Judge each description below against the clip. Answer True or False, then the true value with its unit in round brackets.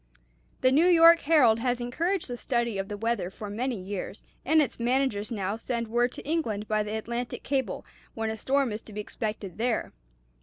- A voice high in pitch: True (235 Hz)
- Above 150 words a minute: True (195 wpm)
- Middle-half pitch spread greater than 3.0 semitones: True (3.7 semitones)